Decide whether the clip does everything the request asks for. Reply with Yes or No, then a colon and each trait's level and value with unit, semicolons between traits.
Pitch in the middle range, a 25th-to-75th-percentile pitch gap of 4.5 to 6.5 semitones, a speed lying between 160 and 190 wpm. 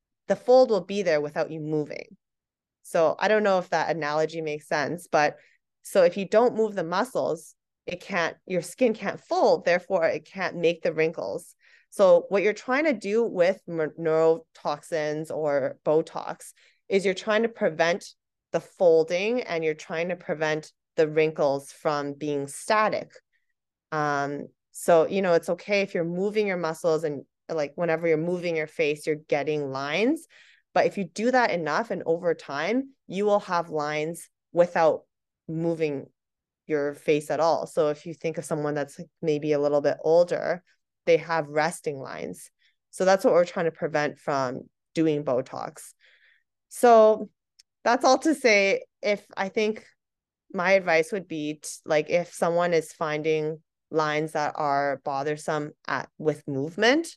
Yes: medium, 170 Hz; average, 5.1 semitones; average, 165 wpm